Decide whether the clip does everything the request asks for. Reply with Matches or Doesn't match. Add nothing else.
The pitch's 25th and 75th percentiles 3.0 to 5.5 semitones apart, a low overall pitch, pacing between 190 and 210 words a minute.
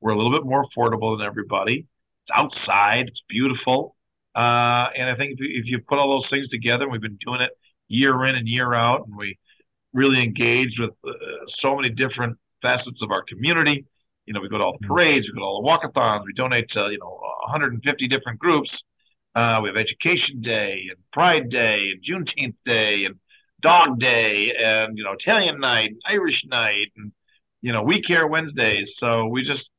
Matches